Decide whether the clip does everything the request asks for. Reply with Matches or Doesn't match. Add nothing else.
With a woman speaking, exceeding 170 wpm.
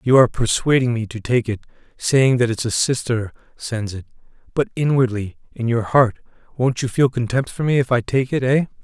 Doesn't match